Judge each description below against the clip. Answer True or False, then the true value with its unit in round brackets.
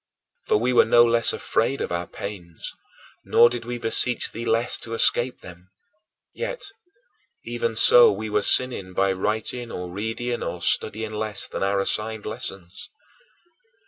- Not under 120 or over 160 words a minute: True (150 wpm)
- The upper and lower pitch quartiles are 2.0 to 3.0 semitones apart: False (3.6 semitones)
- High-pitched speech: False (110 Hz)